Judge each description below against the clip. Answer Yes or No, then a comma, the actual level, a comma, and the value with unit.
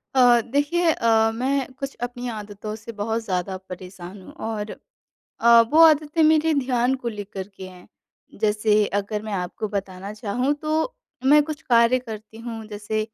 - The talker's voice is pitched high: Yes, high, 225 Hz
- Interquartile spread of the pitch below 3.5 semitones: No, average, 4.2 semitones